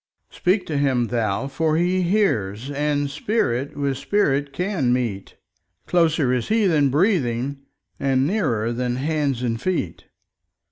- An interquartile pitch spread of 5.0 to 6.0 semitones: Yes, average, 5.3 semitones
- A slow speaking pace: Yes, slow, 130 wpm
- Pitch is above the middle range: No, medium, 140 Hz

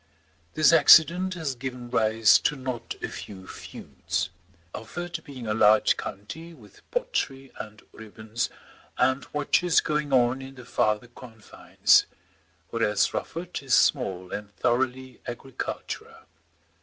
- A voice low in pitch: Yes, low, 125 Hz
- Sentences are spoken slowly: Yes, slow, 120 wpm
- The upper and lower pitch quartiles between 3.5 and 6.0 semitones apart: Yes, average, 5.1 semitones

